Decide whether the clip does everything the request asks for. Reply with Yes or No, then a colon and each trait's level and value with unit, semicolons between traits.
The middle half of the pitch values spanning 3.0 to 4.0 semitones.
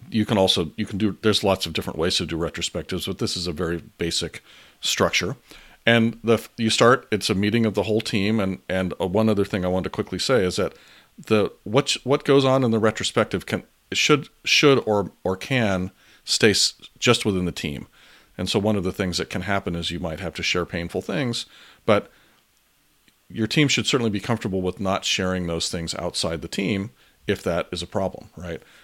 Yes: average, 3.6 semitones